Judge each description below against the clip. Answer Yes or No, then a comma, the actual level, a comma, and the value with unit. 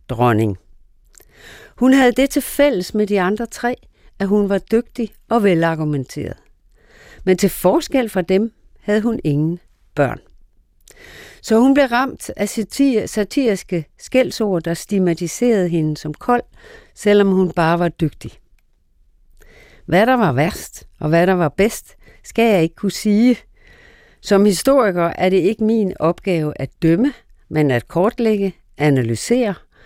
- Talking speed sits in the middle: No, slow, 140 wpm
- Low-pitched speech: No, high, 195 Hz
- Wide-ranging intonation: Yes, wide, 5.7 semitones